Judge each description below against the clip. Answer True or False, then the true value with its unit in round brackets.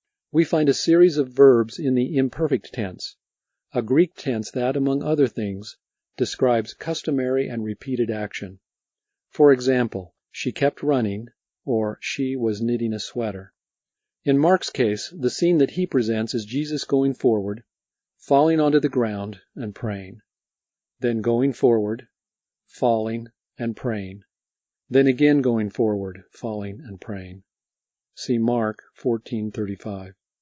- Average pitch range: True (4.4 semitones)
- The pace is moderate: False (130 wpm)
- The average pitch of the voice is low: True (120 Hz)